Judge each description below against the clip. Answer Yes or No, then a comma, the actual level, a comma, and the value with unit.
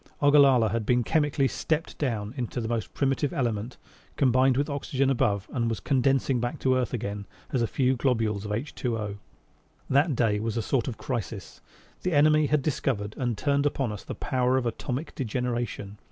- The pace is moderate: Yes, average, 180 wpm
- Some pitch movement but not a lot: Yes, average, 3.4 semitones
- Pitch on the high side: No, low, 125 Hz